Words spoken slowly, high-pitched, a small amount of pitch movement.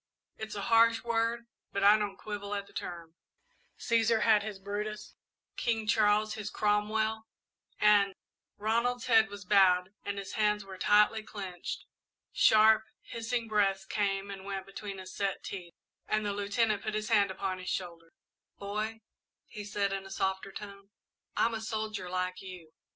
No: average, 160 wpm; high, 205 Hz; narrow, 1.9 semitones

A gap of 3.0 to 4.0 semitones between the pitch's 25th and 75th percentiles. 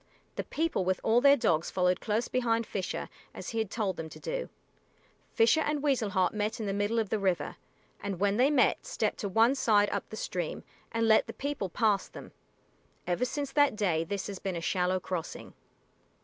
No: average, 4.5 semitones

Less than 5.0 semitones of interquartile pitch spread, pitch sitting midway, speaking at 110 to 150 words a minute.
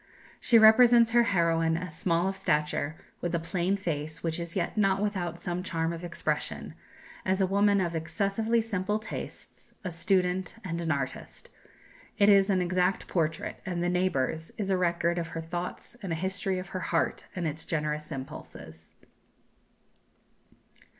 No: average, 2.9 semitones; medium, 175 Hz; average, 165 wpm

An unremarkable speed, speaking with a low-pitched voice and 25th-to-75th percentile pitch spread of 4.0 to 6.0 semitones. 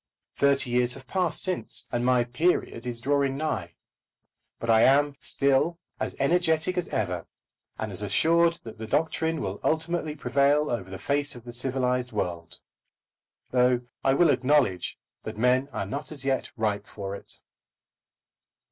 Yes: average, 155 wpm; low, 130 Hz; average, 4.7 semitones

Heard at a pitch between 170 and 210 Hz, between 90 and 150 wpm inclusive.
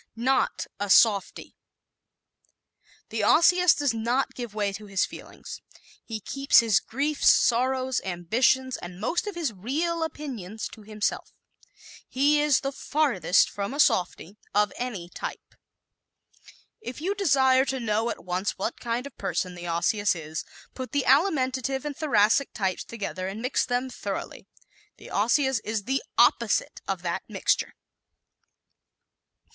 No: high, 240 Hz; average, 140 wpm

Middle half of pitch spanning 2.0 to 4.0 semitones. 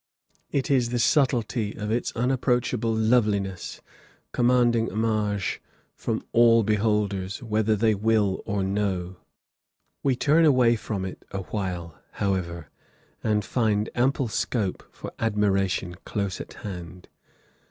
Yes: average, 3.3 semitones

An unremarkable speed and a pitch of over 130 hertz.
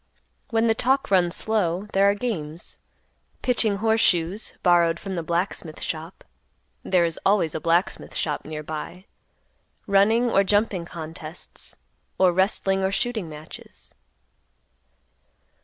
No: slow, 125 wpm; medium, 185 Hz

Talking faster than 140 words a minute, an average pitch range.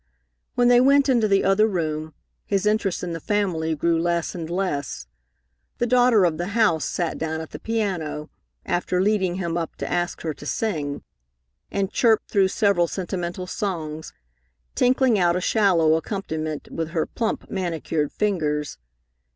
Yes: average, 160 wpm; average, 4.5 semitones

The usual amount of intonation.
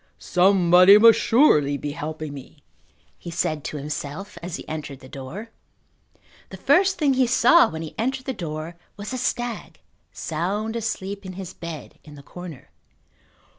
No: wide, 6.5 semitones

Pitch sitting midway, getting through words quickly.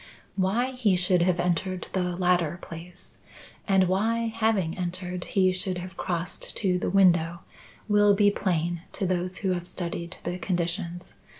No: medium, 180 Hz; average, 155 wpm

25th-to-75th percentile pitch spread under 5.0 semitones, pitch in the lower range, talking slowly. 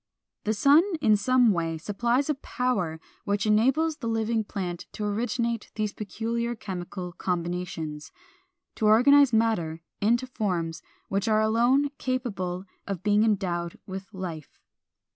No: average, 4.6 semitones; high, 215 Hz; slow, 130 wpm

